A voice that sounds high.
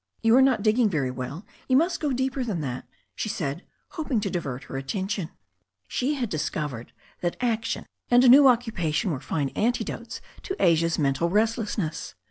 Yes: high, 205 Hz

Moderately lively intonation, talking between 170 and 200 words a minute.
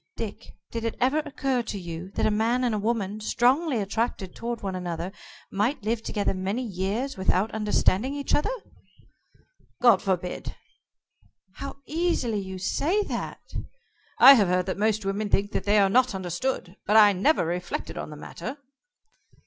No: average, 4.7 semitones; average, 155 wpm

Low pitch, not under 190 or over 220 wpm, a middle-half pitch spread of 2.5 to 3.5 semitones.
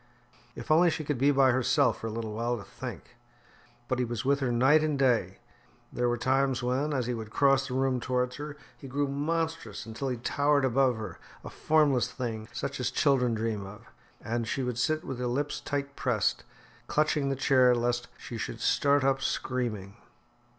Yes: low, 130 Hz; average, 195 wpm; average, 2.8 semitones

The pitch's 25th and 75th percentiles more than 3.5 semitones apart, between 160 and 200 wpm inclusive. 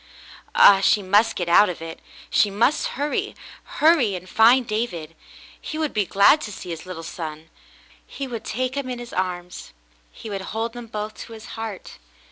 Yes: average, 4.7 semitones; average, 190 wpm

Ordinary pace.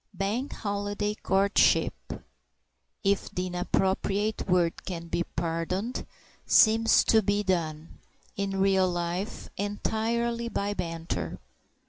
No: slow, 100 wpm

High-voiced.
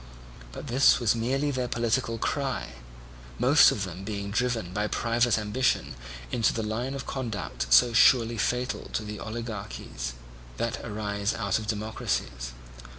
No: low, 115 Hz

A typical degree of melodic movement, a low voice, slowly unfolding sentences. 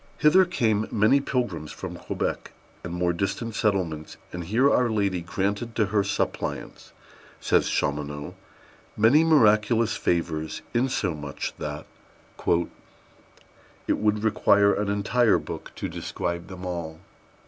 Yes: average, 4.7 semitones; low, 100 Hz; slow, 120 wpm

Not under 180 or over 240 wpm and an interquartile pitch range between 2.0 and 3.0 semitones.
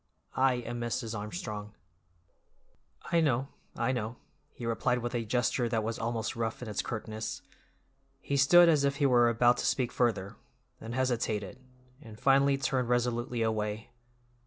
No: average, 155 wpm; narrow, 2.4 semitones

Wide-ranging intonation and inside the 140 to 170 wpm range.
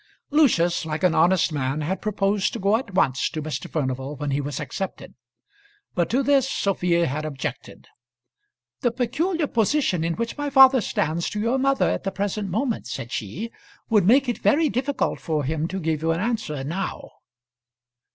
No: wide, 7.4 semitones; average, 180 wpm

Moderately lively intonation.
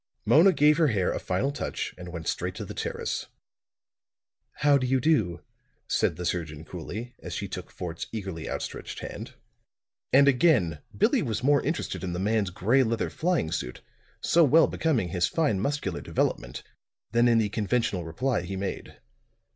No: wide, 7.9 semitones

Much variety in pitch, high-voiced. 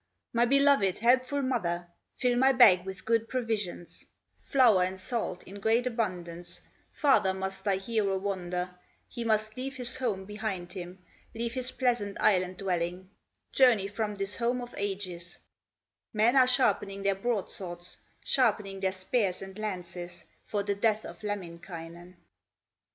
No: average, 4.3 semitones; high, 200 Hz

